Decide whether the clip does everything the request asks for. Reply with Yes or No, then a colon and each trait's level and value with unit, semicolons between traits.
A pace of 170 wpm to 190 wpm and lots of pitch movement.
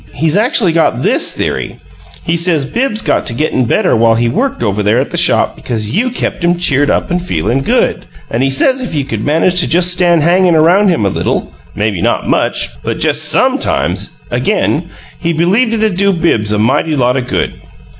No: fast, 205 wpm; wide, 6.8 semitones